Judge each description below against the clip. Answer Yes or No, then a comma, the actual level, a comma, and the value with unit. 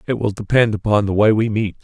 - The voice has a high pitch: No, low, 105 Hz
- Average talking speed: No, fast, 260 wpm